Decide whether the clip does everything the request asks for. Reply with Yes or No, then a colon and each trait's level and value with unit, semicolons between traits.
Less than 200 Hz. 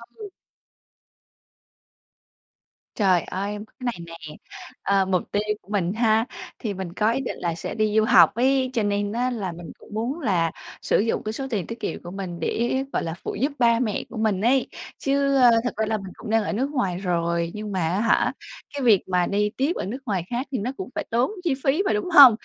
No: high, 215 Hz